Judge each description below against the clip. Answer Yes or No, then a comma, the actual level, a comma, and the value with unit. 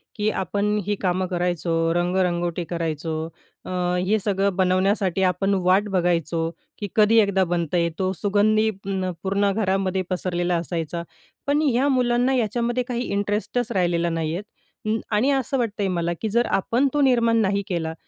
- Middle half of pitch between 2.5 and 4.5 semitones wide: Yes, average, 3.7 semitones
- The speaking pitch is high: Yes, high, 195 Hz